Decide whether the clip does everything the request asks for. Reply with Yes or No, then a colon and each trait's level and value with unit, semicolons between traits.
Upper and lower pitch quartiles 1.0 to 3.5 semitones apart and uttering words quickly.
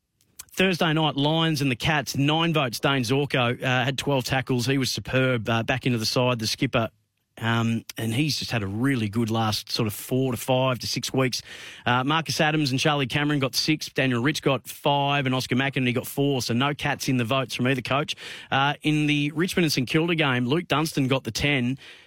Yes: average, 2.9 semitones; fast, 220 wpm